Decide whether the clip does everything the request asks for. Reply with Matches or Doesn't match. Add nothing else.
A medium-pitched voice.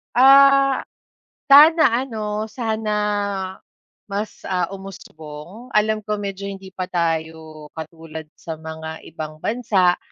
Doesn't match